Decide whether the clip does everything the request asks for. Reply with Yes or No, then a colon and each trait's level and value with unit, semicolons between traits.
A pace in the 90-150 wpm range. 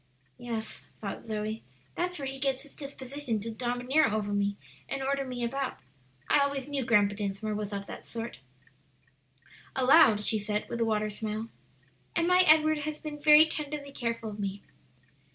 No: average, 170 wpm